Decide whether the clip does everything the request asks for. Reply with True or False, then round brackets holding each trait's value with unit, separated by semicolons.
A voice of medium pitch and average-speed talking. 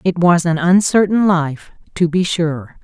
True (175 Hz; 170 wpm)